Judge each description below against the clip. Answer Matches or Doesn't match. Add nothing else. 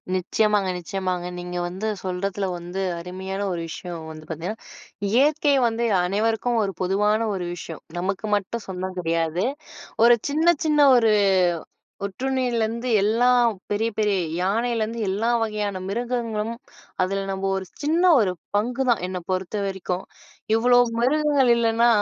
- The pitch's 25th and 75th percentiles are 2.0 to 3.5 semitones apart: Doesn't match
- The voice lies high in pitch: Matches